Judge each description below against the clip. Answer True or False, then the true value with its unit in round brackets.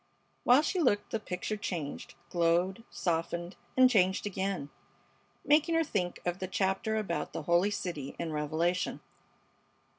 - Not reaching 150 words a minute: True (140 wpm)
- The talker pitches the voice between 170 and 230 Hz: True (185 Hz)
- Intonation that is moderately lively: True (3.8 semitones)